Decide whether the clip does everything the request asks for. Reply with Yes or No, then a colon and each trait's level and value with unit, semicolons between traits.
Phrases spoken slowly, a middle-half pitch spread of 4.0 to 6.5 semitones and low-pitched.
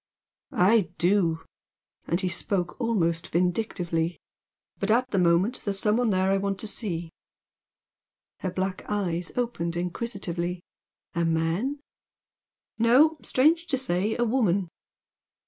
No: slow, 125 wpm; average, 5.0 semitones; high, 195 Hz